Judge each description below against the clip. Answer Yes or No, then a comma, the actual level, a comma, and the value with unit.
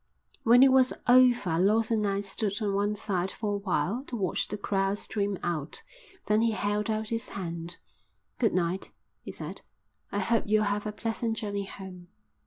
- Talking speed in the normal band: Yes, average, 185 wpm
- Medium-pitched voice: No, high, 205 Hz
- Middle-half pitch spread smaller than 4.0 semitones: Yes, narrow, 2.6 semitones